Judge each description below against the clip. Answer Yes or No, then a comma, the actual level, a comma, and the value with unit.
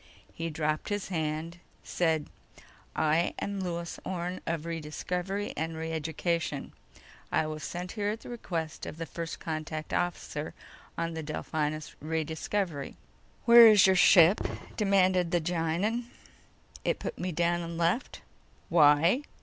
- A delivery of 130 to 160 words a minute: Yes, slow, 135 wpm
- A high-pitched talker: No, medium, 170 Hz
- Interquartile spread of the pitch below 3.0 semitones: Yes, narrow, 2.6 semitones